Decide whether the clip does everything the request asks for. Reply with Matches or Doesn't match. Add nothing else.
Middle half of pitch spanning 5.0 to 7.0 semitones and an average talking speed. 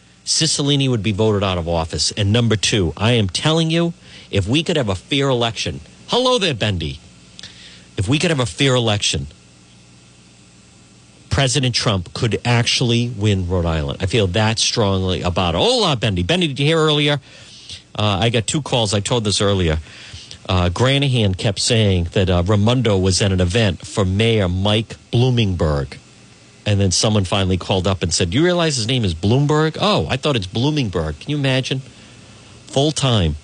Matches